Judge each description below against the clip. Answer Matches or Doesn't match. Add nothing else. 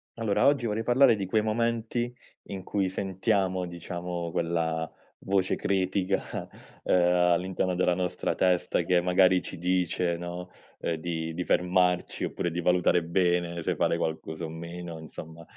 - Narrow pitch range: Matches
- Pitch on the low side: Matches